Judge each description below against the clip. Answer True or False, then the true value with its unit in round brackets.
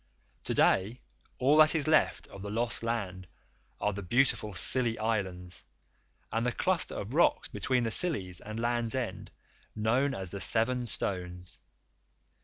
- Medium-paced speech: True (150 wpm)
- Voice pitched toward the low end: True (115 Hz)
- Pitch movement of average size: True (4.5 semitones)